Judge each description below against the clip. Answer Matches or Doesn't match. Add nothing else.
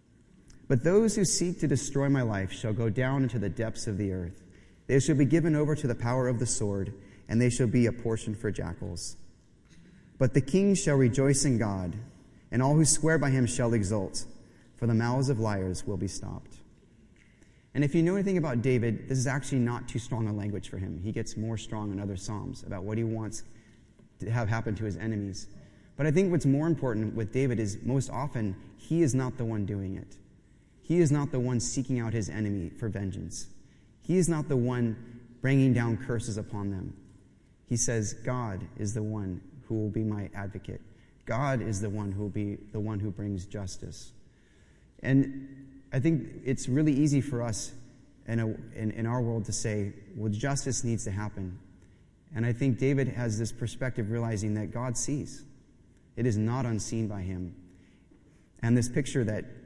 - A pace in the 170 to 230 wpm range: Matches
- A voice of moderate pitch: Doesn't match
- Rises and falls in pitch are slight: Doesn't match